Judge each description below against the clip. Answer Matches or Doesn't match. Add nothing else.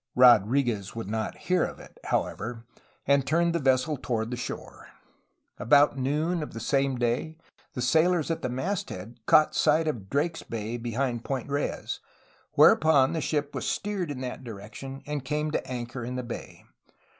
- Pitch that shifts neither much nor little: Matches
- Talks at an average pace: Matches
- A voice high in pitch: Doesn't match